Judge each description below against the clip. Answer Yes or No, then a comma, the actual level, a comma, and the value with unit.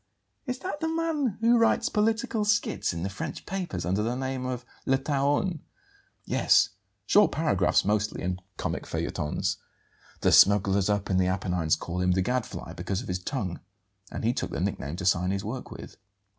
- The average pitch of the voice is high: No, low, 110 Hz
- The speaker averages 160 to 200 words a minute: Yes, average, 180 wpm